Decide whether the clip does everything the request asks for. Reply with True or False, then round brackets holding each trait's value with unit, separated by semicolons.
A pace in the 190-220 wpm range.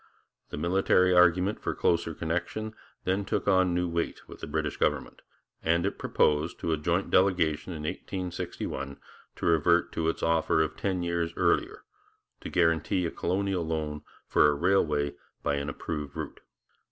False (160 wpm)